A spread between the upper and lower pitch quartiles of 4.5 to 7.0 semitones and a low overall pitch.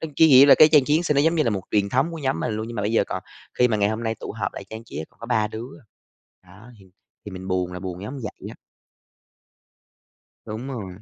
Yes: average, 5.1 semitones; low, 110 Hz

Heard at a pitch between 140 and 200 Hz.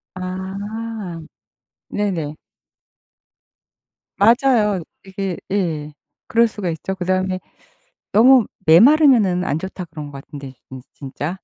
Yes: high, 190 Hz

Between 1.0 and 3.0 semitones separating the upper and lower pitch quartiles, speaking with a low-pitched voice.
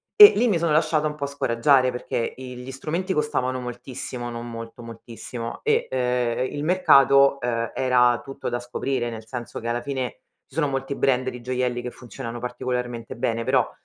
Yes: narrow, 2.4 semitones; low, 125 Hz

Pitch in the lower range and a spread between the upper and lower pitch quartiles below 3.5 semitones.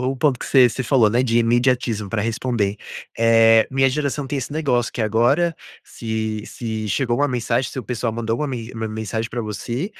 Yes: low, 120 Hz; narrow, 2.6 semitones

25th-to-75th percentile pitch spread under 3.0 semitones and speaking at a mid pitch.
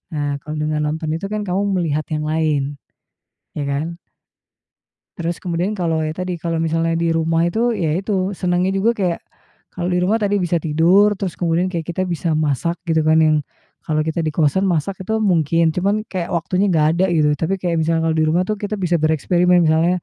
Yes: narrow, 2.6 semitones; medium, 170 Hz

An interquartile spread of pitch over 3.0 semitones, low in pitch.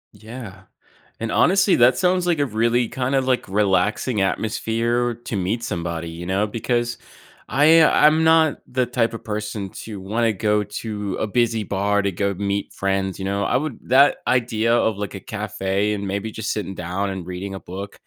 Yes: average, 3.7 semitones; low, 110 Hz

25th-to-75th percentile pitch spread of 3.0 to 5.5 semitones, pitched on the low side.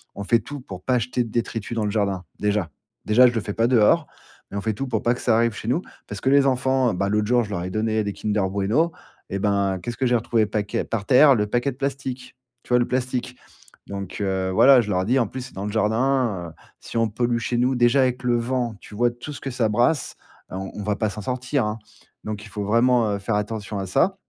Yes: average, 3.5 semitones; low, 115 Hz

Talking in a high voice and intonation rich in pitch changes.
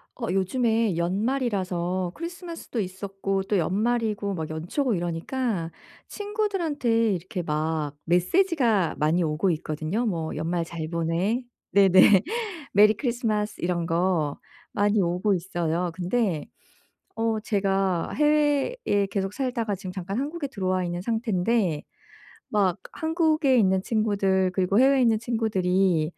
No: high, 195 Hz; average, 4.9 semitones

